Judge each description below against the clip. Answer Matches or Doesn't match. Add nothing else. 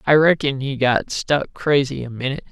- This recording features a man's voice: Matches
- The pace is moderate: Matches